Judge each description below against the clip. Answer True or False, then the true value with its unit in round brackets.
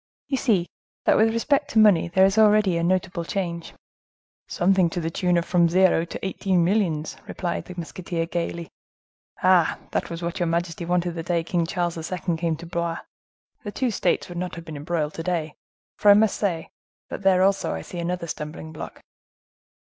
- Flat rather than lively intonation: True (2.1 semitones)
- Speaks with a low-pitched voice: False (175 Hz)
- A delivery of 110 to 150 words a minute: False (195 wpm)